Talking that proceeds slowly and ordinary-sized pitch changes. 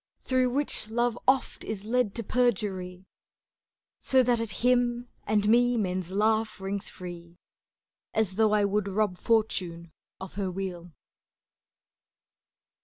Yes: slow, 125 wpm; average, 4.2 semitones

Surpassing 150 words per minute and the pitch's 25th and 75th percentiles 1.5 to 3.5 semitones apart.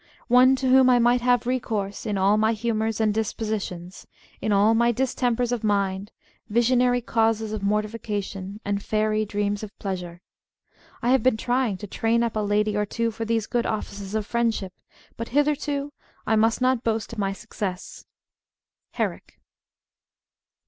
Yes: average, 165 wpm; narrow, 2.6 semitones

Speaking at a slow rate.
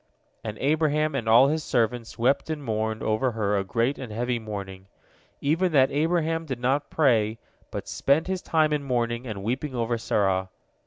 No: average, 175 wpm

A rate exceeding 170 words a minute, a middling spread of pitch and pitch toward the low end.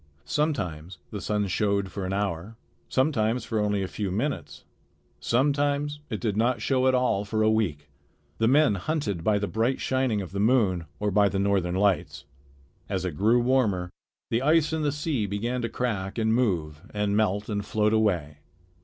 Yes: average, 180 wpm; average, 4.4 semitones; low, 105 Hz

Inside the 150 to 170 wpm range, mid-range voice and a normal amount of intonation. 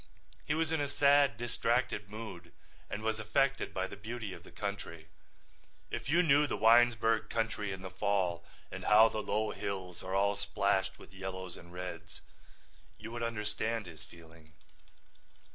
No: average, 160 wpm; low, 105 Hz; average, 3.7 semitones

